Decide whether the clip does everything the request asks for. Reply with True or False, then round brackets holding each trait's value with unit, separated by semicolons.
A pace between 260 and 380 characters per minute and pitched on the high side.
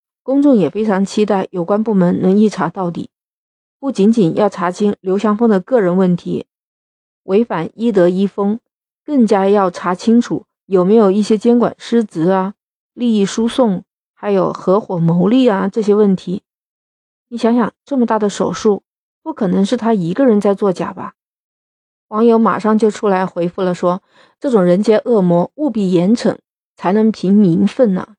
False (245 characters per minute; 205 Hz)